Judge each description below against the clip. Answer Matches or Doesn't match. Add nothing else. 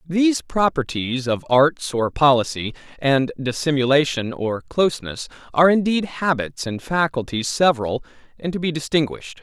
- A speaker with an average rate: Doesn't match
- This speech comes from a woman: Doesn't match